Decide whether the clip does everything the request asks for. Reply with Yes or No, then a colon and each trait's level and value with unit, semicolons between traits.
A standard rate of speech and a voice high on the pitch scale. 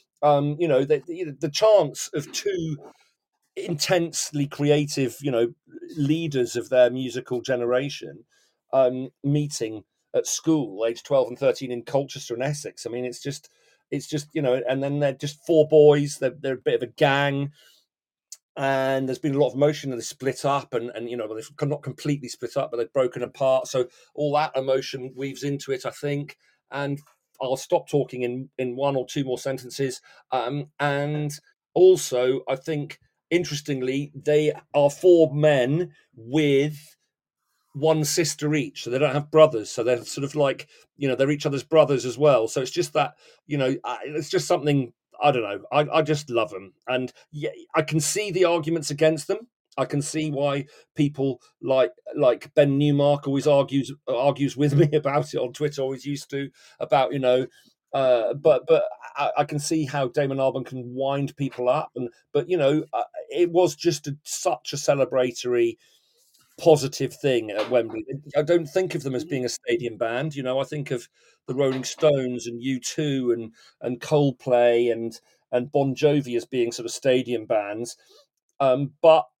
No: average, 185 wpm; medium, 140 Hz